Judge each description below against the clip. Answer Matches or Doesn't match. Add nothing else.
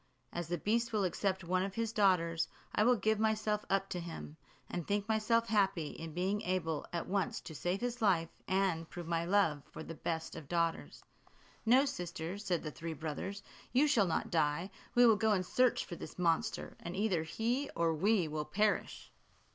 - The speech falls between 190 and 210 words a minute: Matches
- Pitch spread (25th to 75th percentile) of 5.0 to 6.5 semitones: Doesn't match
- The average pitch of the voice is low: Doesn't match